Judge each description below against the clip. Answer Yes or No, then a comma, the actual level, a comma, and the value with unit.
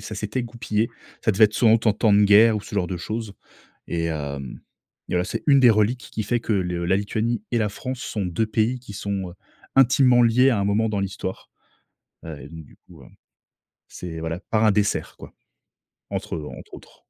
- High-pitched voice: No, low, 105 Hz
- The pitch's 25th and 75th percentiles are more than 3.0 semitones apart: Yes, average, 3.7 semitones